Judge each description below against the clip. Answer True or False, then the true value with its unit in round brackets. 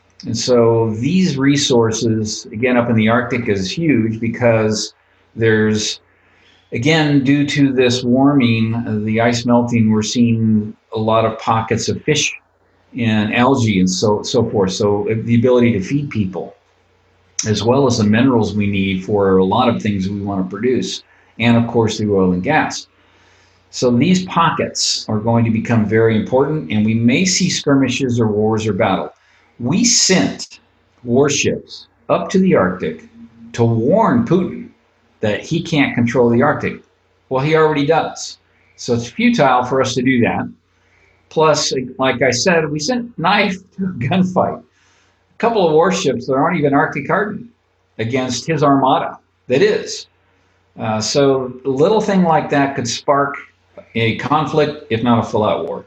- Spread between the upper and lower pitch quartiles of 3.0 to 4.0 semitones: False (4.9 semitones)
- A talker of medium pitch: False (120 Hz)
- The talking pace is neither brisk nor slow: True (160 wpm)